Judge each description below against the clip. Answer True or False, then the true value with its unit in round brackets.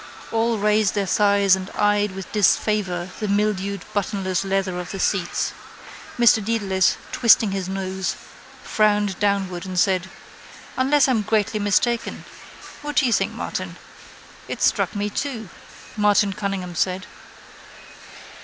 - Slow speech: True (130 wpm)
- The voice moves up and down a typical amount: False (2.1 semitones)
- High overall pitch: True (200 Hz)